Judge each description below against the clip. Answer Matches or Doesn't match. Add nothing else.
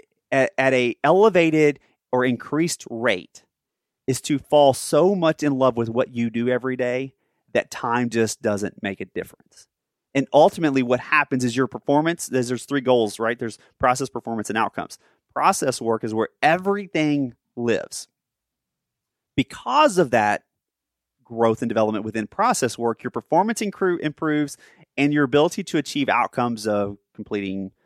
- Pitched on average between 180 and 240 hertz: Doesn't match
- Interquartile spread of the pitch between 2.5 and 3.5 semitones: Doesn't match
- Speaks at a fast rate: Doesn't match